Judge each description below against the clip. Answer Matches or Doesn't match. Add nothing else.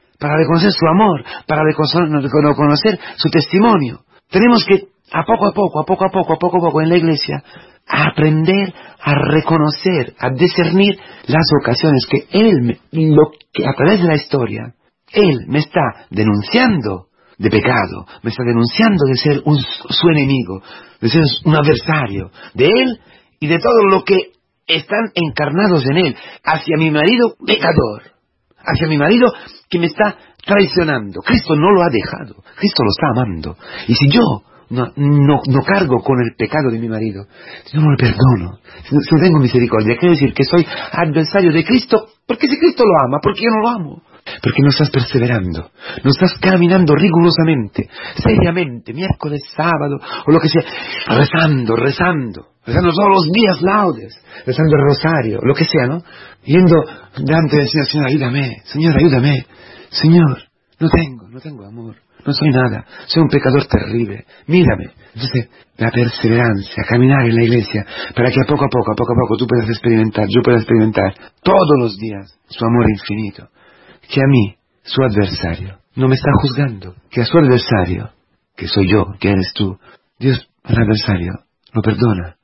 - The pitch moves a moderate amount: Doesn't match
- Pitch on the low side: Doesn't match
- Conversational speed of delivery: Matches